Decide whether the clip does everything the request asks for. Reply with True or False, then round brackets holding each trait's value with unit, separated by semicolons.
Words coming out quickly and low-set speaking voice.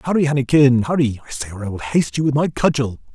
True (250 wpm; 130 Hz)